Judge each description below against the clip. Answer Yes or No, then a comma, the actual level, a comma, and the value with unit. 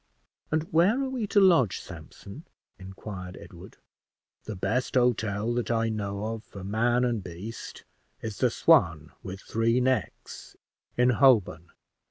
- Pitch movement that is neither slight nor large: Yes, average, 4.1 semitones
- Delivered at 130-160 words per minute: Yes, average, 140 wpm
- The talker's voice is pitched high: No, low, 115 Hz